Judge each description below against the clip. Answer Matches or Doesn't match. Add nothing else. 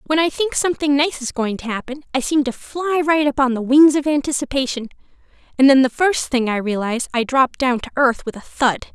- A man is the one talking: Doesn't match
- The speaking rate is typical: Doesn't match